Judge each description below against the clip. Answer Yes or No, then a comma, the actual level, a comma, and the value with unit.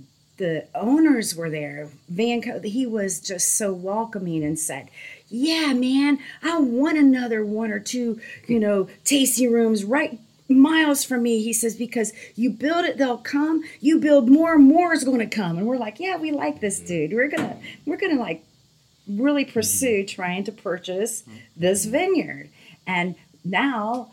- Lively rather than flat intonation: Yes, wide, 6.9 semitones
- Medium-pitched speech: No, high, 230 Hz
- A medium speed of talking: Yes, average, 170 wpm